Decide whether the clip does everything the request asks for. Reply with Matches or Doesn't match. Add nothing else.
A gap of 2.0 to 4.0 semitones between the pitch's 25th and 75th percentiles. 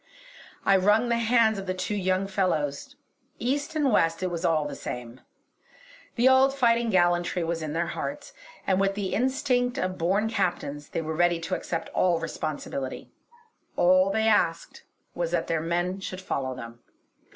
Doesn't match